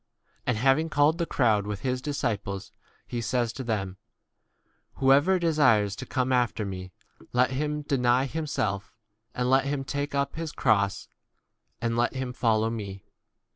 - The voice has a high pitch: No, low, 125 Hz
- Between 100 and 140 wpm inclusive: No, average, 155 wpm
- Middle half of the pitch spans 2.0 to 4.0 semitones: No, average, 4.7 semitones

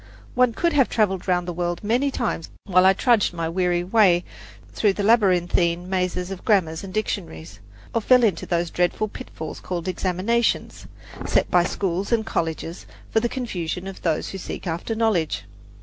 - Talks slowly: No, average, 170 wpm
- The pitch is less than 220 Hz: Yes, medium, 185 Hz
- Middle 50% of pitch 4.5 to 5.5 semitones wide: No, average, 3.9 semitones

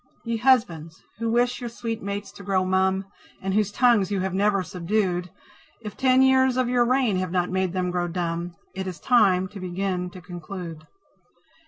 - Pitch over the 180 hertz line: Yes, high, 190 Hz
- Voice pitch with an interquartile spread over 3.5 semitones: Yes, average, 4.2 semitones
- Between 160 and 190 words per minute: Yes, average, 185 wpm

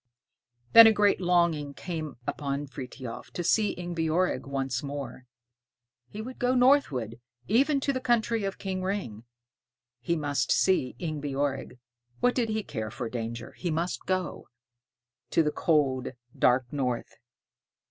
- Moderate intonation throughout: No, wide, 7.0 semitones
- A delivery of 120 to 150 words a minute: Yes, slow, 135 wpm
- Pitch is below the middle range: No, medium, 155 Hz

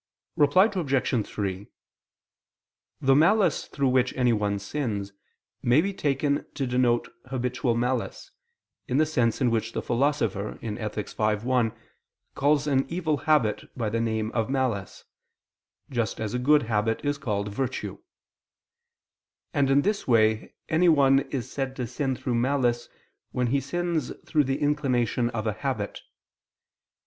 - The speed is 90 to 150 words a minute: Yes, average, 140 wpm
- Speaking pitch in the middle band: No, low, 125 Hz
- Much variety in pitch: No, average, 4.0 semitones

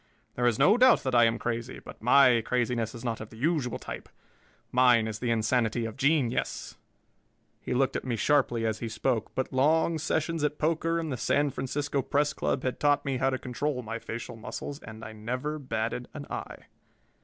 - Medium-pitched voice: No, low, 125 Hz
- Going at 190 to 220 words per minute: Yes, average, 200 wpm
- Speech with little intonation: No, average, 3.9 semitones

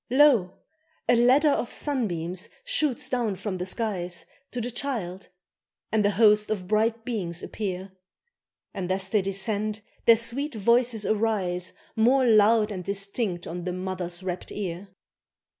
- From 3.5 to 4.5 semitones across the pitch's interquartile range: Yes, average, 4.0 semitones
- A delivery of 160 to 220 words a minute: No, average, 140 wpm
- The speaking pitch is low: No, high, 210 Hz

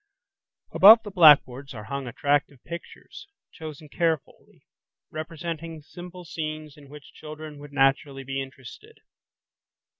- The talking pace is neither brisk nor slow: No, slow, 115 wpm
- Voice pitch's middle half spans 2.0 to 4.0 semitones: Yes, average, 2.9 semitones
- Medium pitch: Yes, medium, 150 Hz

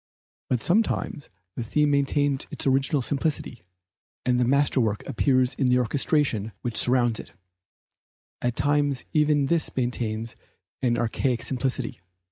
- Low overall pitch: Yes, low, 130 Hz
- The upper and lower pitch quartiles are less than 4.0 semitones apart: Yes, average, 3.0 semitones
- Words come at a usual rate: No, slow, 125 wpm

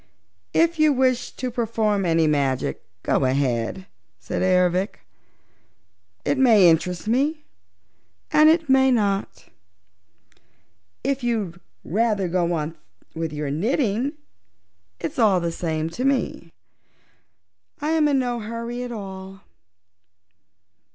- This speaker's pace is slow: Yes, slow, 115 wpm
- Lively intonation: Yes, wide, 7.2 semitones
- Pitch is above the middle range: Yes, high, 210 Hz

